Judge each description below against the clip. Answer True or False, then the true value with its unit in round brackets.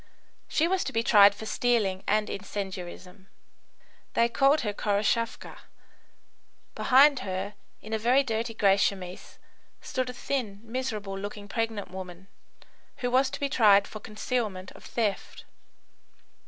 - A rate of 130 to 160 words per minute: True (135 wpm)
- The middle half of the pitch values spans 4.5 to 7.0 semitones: False (3.7 semitones)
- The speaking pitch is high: True (215 Hz)